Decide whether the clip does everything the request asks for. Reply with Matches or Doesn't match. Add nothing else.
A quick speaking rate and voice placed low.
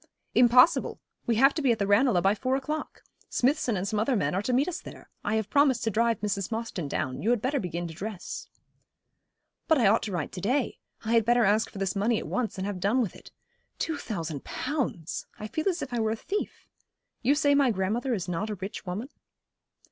Doesn't match